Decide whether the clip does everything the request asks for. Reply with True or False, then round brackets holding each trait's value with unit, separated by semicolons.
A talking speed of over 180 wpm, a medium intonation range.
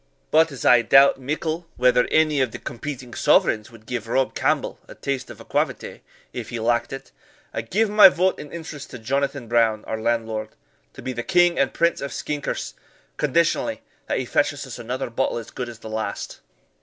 True (195 wpm; 4.3 semitones)